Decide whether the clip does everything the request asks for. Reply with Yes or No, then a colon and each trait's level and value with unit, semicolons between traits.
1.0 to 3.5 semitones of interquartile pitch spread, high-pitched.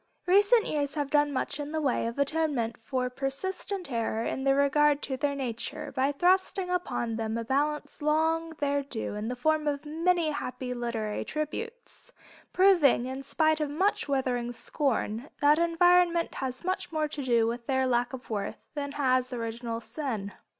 No: average, 4.1 semitones; very high, 280 Hz